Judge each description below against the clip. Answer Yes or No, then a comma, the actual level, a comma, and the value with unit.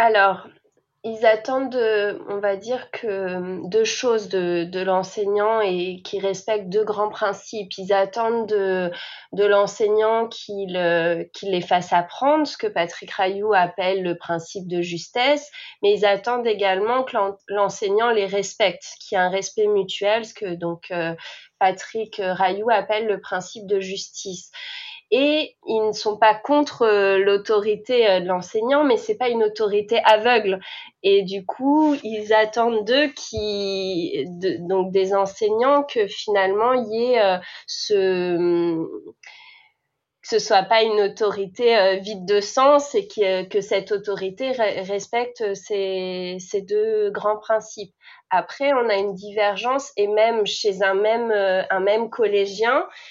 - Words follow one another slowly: Yes, slow, 140 wpm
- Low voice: No, high, 205 Hz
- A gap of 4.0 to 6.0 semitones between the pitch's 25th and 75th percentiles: No, average, 2.9 semitones